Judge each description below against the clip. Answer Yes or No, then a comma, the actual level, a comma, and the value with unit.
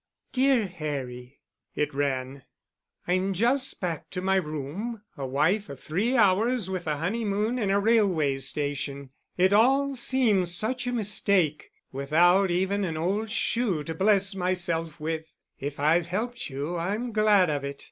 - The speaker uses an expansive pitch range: Yes, wide, 5.9 semitones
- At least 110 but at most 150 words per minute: Yes, average, 145 wpm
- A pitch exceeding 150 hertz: Yes, medium, 185 Hz